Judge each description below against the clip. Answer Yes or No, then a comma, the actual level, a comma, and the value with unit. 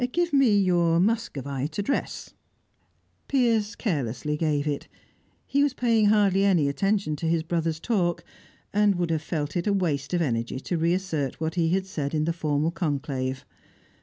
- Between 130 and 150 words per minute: No, average, 160 wpm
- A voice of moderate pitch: Yes, medium, 170 Hz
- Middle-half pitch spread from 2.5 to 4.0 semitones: No, average, 5.2 semitones